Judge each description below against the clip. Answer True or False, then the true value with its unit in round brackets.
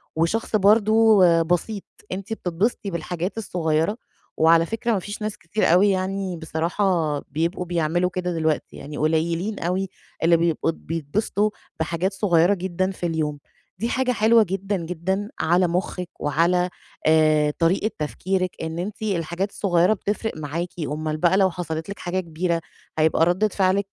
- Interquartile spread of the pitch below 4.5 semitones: True (3.4 semitones)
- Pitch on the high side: False (180 Hz)